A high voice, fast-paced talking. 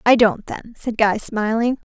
No: high, 225 Hz; average, 190 wpm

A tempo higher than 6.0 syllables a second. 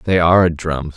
No: 4.4 syllables/s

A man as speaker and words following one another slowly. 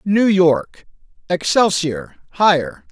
Yes: male; slow, 60 wpm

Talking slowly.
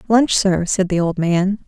No: fast, 215 wpm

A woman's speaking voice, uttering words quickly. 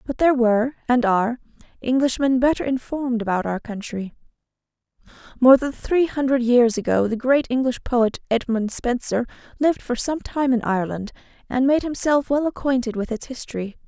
No: female; average, 160 wpm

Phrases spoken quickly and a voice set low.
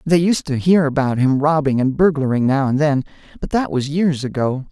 No: fast, 215 wpm; medium, 145 Hz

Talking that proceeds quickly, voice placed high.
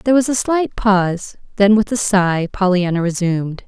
No: average, 180 wpm; high, 200 Hz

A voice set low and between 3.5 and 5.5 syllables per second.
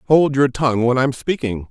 Yes: low, 130 Hz; 5.3 syllables/s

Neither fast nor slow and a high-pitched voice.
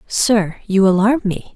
Yes: average, 155 wpm; high, 205 Hz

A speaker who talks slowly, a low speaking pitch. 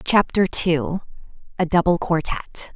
No: slow, 85 wpm; medium, 175 Hz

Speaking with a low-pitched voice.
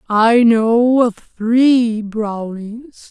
No: high, 230 Hz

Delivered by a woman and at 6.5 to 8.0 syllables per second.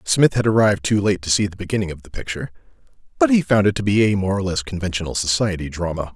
No: male; 6.9 syllables/s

